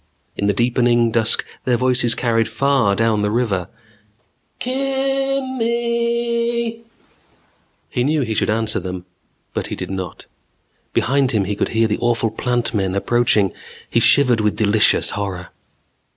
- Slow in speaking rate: No, average, 145 wpm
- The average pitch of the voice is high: No, low, 120 Hz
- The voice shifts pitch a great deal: Yes, wide, 6.7 semitones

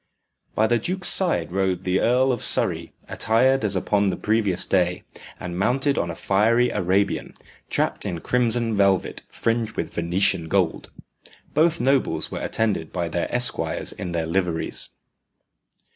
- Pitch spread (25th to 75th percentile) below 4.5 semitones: No, average, 5.1 semitones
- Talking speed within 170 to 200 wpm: No, average, 145 wpm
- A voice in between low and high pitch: No, low, 100 Hz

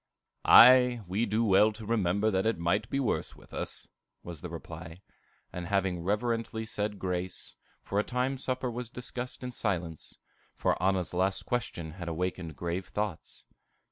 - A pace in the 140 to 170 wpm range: Yes, average, 160 wpm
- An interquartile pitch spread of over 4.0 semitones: Yes, average, 4.6 semitones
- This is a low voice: Yes, low, 100 Hz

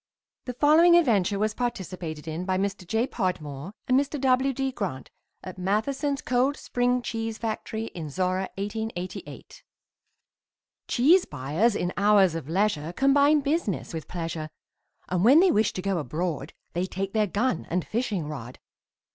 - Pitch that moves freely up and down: Yes, wide, 6.1 semitones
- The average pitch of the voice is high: Yes, high, 200 Hz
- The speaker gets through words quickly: No, average, 150 wpm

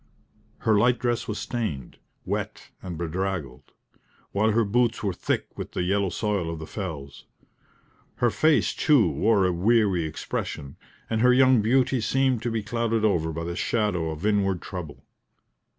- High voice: No, low, 105 Hz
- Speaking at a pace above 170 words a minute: No, average, 160 wpm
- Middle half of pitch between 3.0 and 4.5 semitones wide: No, average, 5.1 semitones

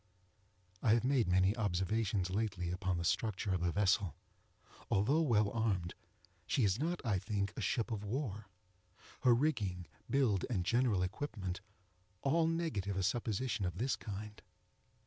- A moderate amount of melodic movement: Yes, average, 4.3 semitones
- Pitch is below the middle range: Yes, low, 105 Hz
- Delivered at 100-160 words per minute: Yes, average, 145 wpm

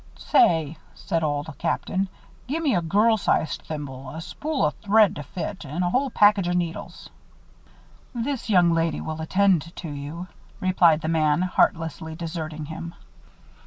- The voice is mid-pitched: Yes, medium, 170 Hz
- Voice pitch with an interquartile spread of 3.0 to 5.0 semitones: Yes, average, 3.8 semitones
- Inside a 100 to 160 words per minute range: Yes, average, 150 wpm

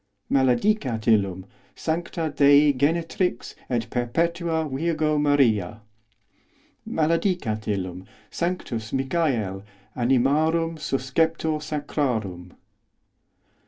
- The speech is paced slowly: Yes, slow, 90 wpm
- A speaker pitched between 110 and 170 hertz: Yes, medium, 140 Hz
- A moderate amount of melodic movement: No, wide, 6.2 semitones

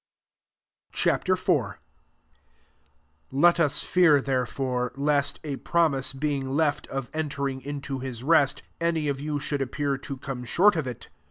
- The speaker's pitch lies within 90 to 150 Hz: Yes, medium, 140 Hz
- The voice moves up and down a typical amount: No, narrow, 2.2 semitones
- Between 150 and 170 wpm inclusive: No, average, 140 wpm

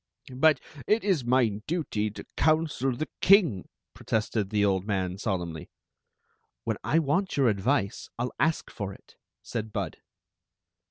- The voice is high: No, low, 120 Hz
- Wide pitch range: Yes, wide, 7.4 semitones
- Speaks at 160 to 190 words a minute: No, average, 145 wpm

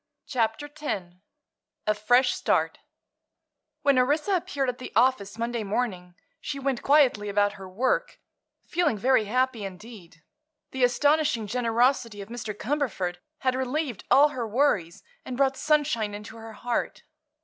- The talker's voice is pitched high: Yes, high, 245 Hz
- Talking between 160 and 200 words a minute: No, average, 140 wpm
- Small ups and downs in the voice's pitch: No, average, 4.7 semitones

